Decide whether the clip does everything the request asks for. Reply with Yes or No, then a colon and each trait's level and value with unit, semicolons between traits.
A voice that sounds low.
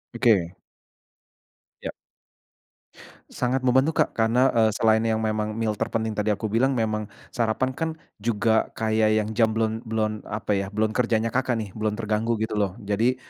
Yes: low, 110 Hz